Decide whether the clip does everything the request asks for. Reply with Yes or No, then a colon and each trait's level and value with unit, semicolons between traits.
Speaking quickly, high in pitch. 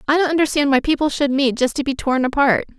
Yes: fast, 260 wpm; very high, 280 Hz